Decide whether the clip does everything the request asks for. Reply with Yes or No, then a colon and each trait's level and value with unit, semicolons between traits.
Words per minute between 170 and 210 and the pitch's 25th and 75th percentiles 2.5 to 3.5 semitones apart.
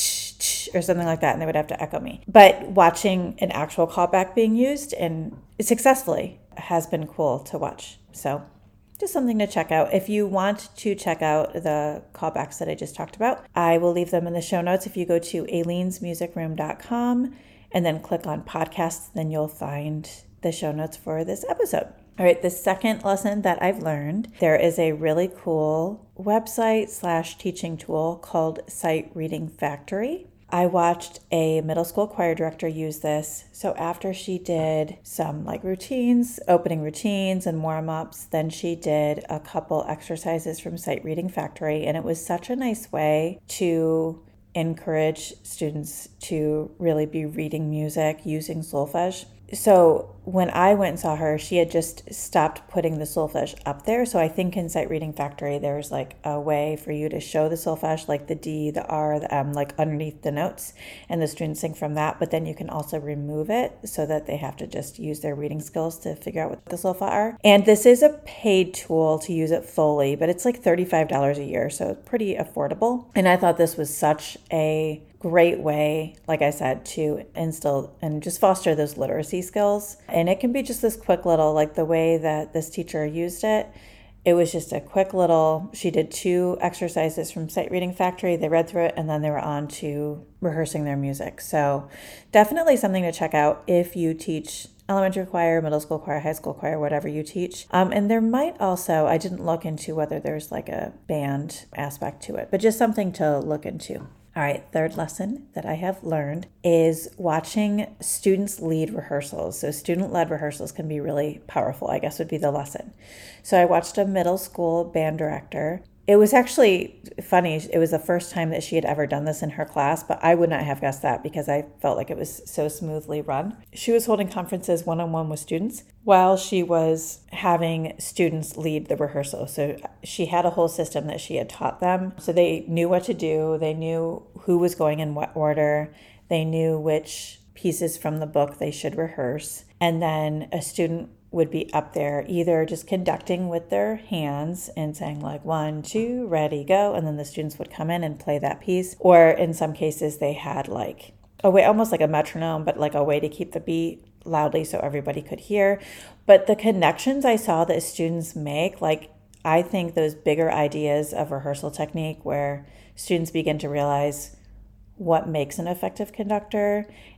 Yes: average, 195 wpm; average, 3.0 semitones